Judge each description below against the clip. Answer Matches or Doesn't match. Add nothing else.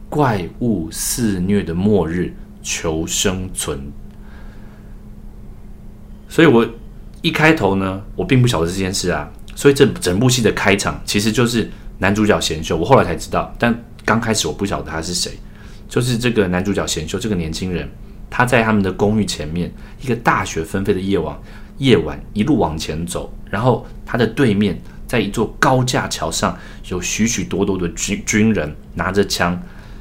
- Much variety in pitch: Doesn't match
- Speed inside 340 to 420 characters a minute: Doesn't match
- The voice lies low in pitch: Matches